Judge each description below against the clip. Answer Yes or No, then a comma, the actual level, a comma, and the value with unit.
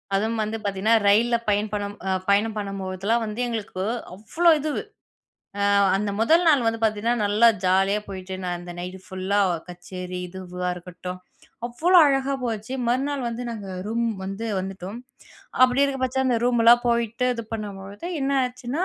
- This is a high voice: Yes, high, 215 Hz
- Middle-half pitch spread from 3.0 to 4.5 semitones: Yes, average, 3.8 semitones